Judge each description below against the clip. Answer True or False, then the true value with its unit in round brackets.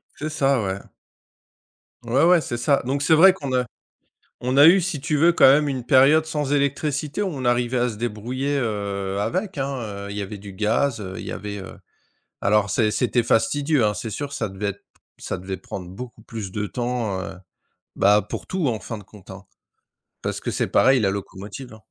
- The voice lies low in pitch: True (120 Hz)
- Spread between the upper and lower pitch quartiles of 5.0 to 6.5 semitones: True (5.5 semitones)